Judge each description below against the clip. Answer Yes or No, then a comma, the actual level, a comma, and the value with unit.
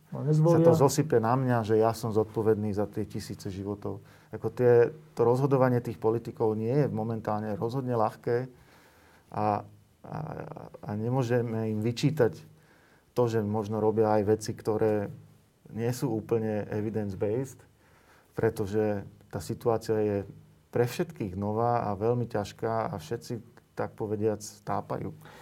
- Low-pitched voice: Yes, low, 110 Hz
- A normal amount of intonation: No, narrow, 2.2 semitones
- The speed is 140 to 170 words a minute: No, average, 130 wpm